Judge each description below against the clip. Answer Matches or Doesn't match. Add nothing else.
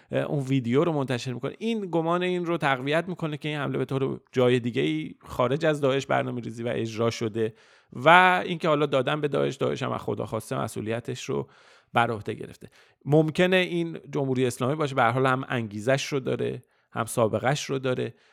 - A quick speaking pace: Matches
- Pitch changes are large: Doesn't match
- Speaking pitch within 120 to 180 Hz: Matches